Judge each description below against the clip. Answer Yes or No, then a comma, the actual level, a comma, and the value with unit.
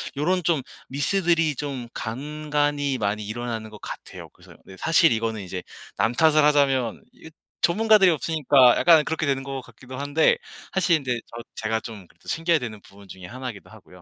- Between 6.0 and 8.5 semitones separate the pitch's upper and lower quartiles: No, wide, 5.6 semitones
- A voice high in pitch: No, low, 135 Hz